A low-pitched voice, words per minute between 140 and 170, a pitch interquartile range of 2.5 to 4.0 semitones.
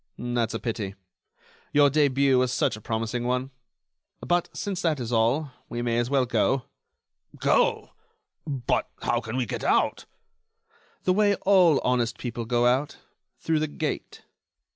Yes: low, 125 Hz; average, 150 wpm; average, 3.7 semitones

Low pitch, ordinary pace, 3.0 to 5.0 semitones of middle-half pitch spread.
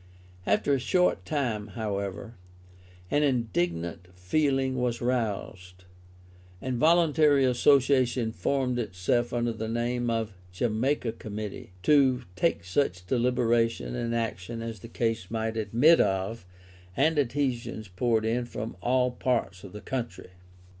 No: low, 120 Hz; slow, 125 wpm; average, 3.4 semitones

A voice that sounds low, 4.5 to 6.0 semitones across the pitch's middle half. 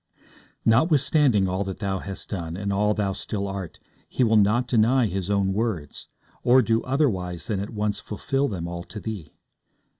No: low, 105 Hz; average, 3.0 semitones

